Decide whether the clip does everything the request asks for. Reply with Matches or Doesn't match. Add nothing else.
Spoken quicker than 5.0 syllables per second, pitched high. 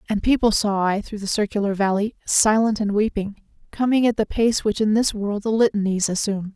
Matches